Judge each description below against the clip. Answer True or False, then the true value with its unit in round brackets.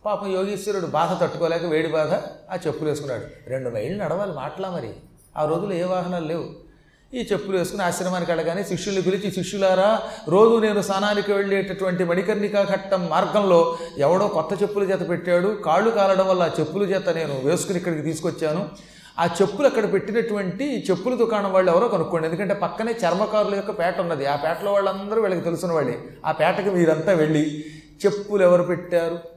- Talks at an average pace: False (155 wpm)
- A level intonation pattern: False (3.2 semitones)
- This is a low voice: False (185 Hz)